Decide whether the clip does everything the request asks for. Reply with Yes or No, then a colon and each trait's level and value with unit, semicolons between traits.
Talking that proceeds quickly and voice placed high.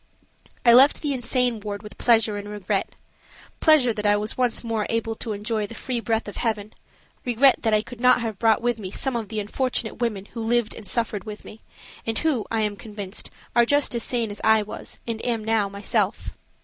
Yes: fast, 210 wpm; high, 225 Hz